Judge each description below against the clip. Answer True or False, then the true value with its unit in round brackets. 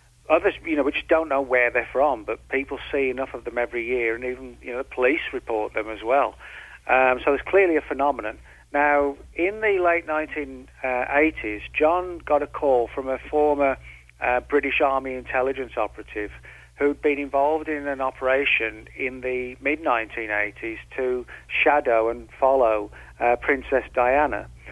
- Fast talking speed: False (160 wpm)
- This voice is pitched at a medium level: False (130 Hz)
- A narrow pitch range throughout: False (3.2 semitones)